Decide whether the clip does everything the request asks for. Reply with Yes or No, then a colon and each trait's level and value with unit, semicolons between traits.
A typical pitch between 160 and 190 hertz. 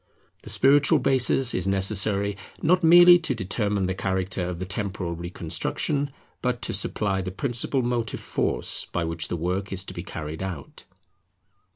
No: low, 100 Hz